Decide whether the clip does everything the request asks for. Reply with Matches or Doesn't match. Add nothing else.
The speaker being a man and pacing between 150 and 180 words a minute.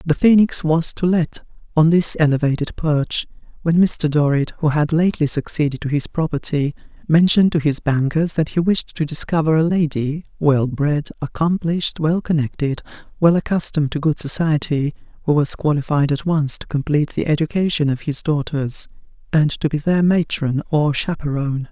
Doesn't match